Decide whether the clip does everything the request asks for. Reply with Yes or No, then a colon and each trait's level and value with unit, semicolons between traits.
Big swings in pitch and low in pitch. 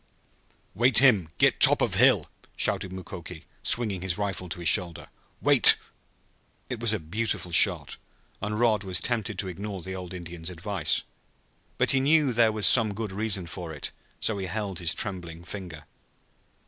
No: average, 3.8 semitones; very low, 95 Hz